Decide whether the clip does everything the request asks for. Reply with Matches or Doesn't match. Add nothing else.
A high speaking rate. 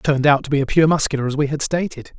Matches